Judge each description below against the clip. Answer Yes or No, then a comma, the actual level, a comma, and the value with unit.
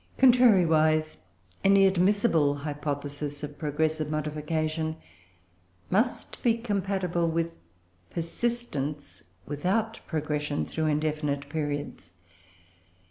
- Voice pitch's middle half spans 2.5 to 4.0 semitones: No, average, 4.5 semitones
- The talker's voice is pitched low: No, medium, 155 Hz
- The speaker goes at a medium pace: No, slow, 80 wpm